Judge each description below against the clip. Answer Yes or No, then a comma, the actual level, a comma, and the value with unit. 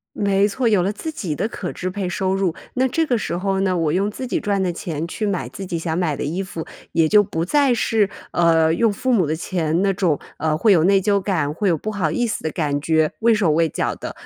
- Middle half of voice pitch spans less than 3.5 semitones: No, average, 4.1 semitones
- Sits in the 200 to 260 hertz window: No, medium, 185 Hz